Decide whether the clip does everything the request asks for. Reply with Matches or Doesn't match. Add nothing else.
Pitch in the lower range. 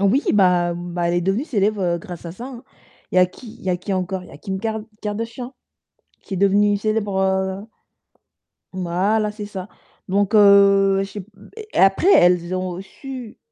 Doesn't match